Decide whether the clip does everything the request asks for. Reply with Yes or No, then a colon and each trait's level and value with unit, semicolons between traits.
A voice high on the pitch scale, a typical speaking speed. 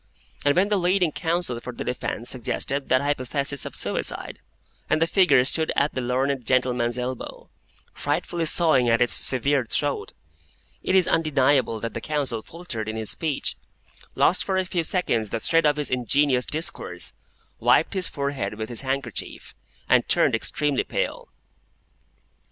No: medium, 140 Hz; average, 155 wpm